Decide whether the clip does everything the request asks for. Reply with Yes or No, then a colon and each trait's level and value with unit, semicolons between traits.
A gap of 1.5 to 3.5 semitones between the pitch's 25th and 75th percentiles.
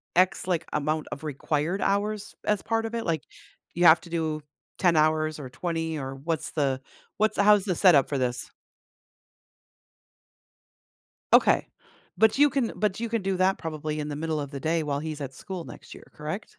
No: average, 4.5 semitones